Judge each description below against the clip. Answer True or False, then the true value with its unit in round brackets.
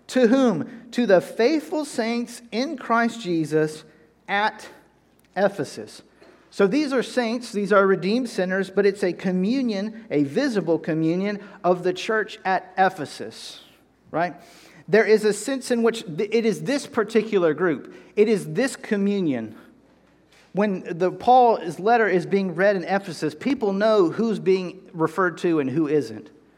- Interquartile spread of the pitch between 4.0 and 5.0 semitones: True (4.6 semitones)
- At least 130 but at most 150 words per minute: True (145 wpm)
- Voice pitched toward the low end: False (200 Hz)